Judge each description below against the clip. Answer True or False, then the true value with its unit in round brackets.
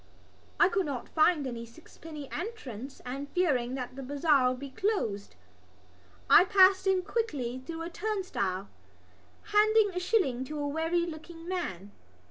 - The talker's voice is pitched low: False (310 Hz)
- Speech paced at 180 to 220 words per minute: False (145 wpm)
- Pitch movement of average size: False (6.3 semitones)